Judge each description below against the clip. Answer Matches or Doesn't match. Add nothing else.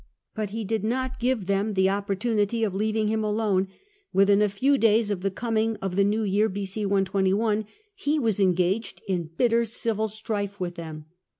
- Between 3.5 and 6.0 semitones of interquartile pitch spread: Doesn't match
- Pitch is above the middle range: Matches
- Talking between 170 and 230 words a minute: Matches